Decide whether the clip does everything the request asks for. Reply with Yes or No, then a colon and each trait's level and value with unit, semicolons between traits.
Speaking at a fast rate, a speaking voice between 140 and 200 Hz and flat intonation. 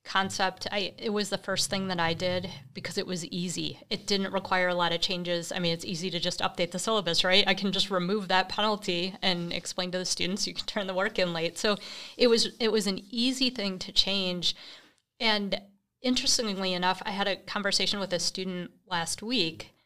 Yes: fast, 215 wpm; high, 190 Hz; narrow, 2.0 semitones